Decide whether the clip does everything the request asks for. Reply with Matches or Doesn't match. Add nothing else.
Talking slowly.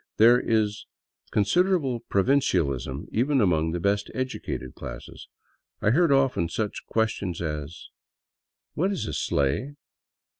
Matches